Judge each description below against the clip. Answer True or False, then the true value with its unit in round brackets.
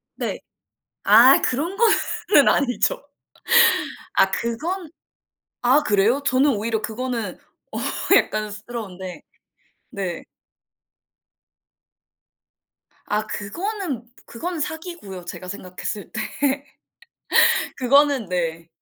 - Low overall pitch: False (235 Hz)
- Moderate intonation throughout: False (6.3 semitones)